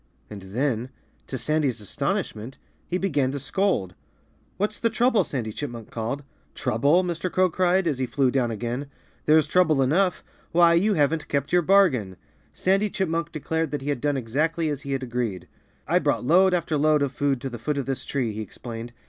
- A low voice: No, medium, 145 Hz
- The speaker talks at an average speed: Yes, average, 190 wpm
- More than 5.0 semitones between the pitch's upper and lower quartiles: Yes, wide, 5.5 semitones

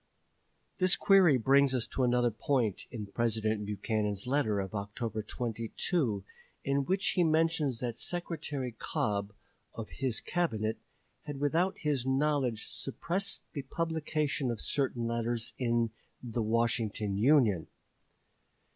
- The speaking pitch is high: No, low, 125 Hz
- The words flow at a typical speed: No, slow, 120 wpm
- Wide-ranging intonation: No, average, 5.0 semitones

